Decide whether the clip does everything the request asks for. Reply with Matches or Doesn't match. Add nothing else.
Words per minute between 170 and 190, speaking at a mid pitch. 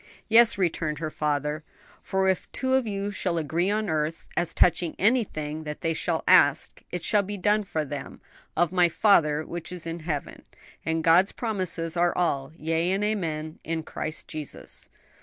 Matches